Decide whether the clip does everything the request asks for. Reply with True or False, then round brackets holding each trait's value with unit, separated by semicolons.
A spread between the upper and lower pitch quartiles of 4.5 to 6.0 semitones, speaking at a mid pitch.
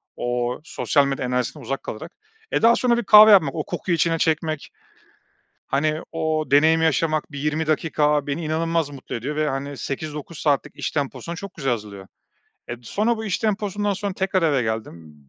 False (3.6 semitones; 155 Hz)